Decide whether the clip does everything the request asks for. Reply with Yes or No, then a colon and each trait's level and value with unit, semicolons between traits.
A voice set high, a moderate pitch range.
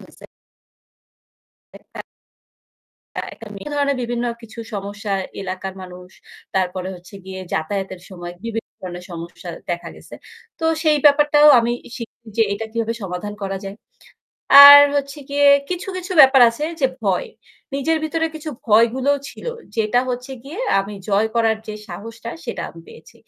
No: high, 225 Hz; wide, 6.5 semitones